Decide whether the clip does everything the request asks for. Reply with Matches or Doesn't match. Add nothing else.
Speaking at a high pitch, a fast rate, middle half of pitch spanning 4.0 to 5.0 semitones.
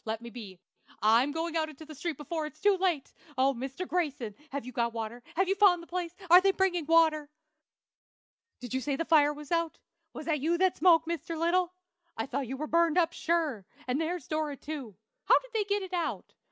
Matches